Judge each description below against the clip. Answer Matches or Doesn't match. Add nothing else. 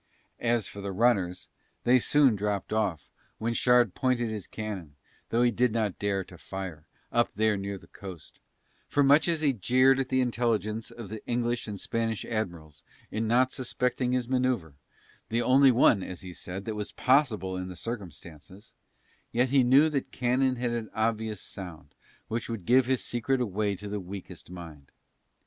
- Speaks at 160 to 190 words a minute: Matches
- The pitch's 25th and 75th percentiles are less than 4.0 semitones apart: Doesn't match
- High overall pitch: Doesn't match